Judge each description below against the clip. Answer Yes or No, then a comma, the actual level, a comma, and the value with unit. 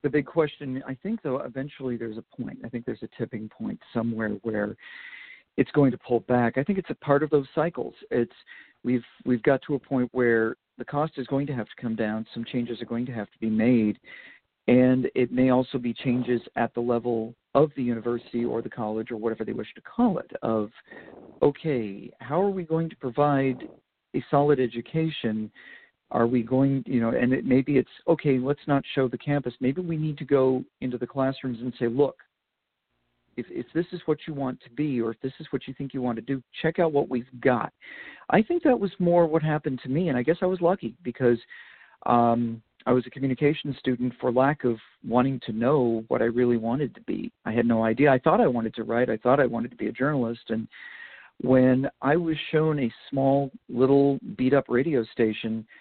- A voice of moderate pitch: No, low, 130 Hz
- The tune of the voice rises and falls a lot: No, average, 3.4 semitones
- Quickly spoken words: Yes, fast, 220 wpm